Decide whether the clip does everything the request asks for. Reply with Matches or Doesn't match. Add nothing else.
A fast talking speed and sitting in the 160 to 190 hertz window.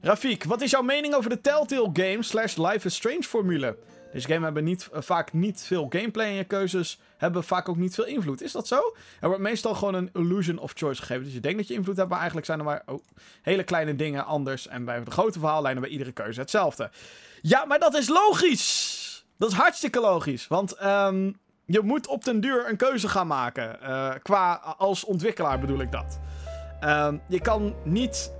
Matches